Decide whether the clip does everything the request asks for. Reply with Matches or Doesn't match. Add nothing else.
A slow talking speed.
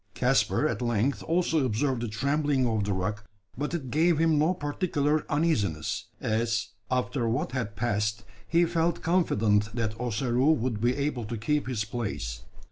Doesn't match